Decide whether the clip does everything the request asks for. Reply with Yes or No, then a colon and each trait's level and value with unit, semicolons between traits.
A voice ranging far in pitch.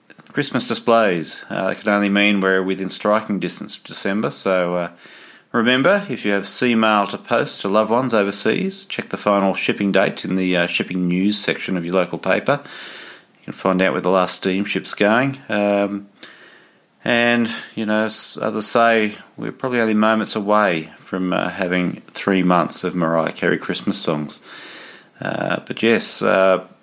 No: average, 2.7 semitones